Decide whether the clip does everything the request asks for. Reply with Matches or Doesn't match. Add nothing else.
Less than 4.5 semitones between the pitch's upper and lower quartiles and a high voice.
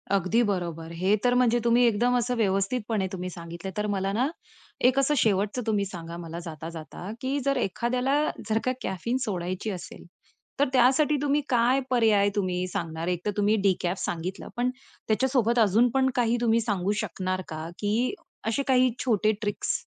Doesn't match